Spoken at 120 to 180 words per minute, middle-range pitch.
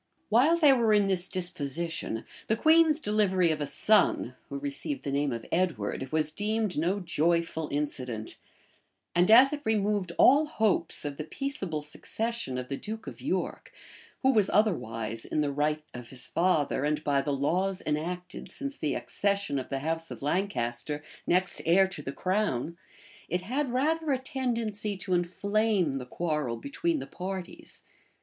Yes: average, 165 wpm; medium, 180 Hz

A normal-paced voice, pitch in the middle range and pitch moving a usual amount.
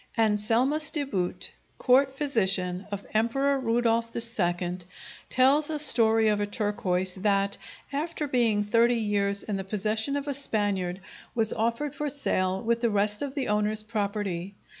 No: average, 150 wpm; high, 220 Hz; average, 4.4 semitones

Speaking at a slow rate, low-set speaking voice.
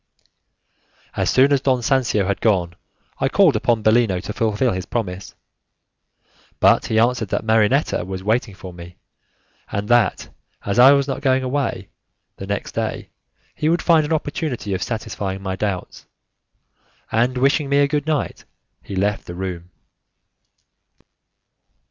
No: average, 150 wpm; low, 115 Hz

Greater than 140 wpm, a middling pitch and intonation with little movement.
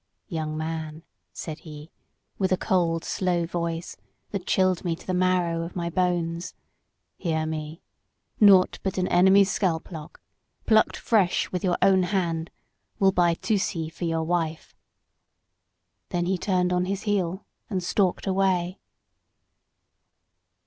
No: slow, 135 wpm; medium, 175 Hz; narrow, 2.2 semitones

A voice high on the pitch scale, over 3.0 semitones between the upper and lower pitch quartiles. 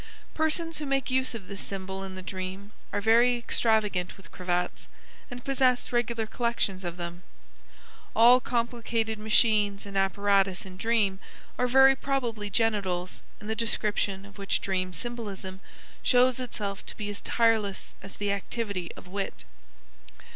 Yes: high, 210 Hz; average, 3.6 semitones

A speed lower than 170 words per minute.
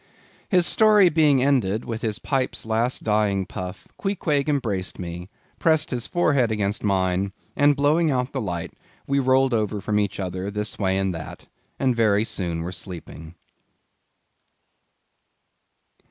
Yes: average, 140 wpm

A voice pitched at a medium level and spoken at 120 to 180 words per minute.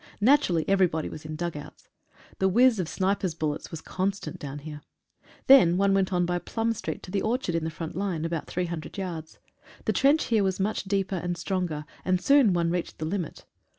No: medium, 180 Hz; fast, 205 wpm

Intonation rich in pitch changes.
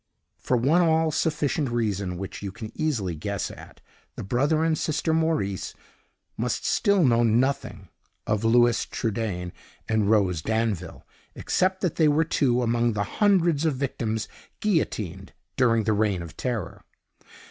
Yes: wide, 7.1 semitones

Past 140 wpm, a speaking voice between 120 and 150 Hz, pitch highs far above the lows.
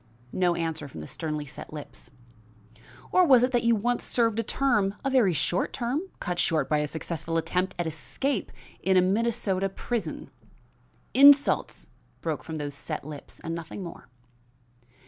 No: average, 165 wpm; medium, 185 Hz; wide, 6.7 semitones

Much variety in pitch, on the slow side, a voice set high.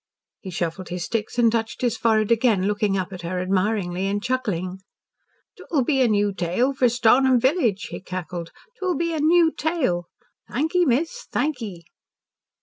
No: wide, 6.0 semitones; average, 170 wpm; high, 220 Hz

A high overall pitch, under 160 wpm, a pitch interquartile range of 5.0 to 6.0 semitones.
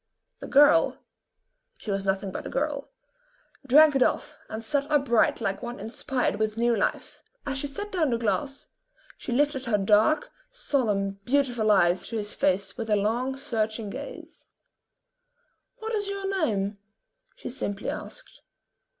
Yes: high, 240 Hz; average, 150 wpm; wide, 5.6 semitones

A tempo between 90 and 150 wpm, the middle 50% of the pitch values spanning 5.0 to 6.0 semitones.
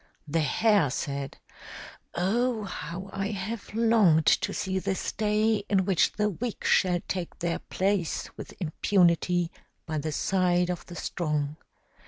No: average, 140 wpm; average, 3.7 semitones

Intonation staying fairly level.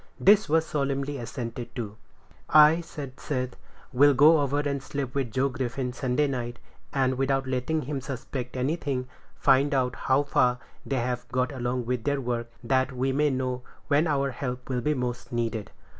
Yes: narrow, 2.2 semitones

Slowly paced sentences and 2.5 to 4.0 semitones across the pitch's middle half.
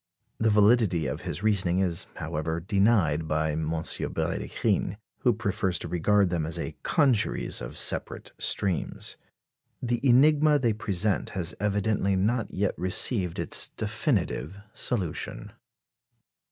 No: slow, 125 wpm; average, 4.5 semitones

